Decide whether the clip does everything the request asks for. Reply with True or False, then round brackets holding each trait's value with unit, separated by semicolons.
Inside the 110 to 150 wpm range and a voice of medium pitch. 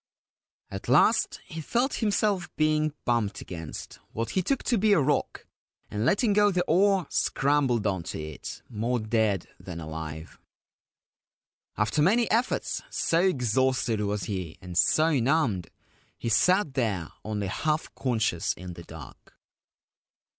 False (140 wpm; 125 Hz)